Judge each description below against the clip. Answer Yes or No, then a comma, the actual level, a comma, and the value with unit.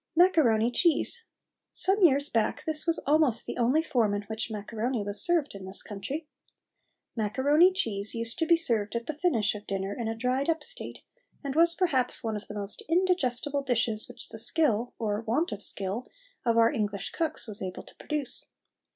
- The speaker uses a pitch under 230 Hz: No, high, 240 Hz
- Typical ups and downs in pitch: No, wide, 6.6 semitones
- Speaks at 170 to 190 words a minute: Yes, average, 185 wpm